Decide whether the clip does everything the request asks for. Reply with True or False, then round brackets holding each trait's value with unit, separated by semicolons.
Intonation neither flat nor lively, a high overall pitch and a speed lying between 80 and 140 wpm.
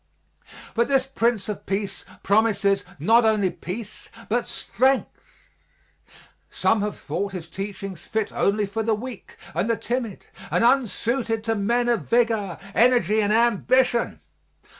True (3.0 semitones; 220 Hz; 135 wpm)